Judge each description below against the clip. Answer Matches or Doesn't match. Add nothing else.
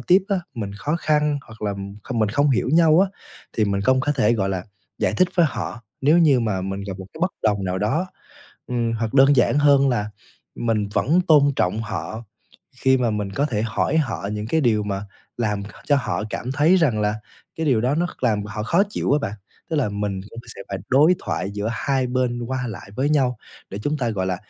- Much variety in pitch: Matches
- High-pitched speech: Doesn't match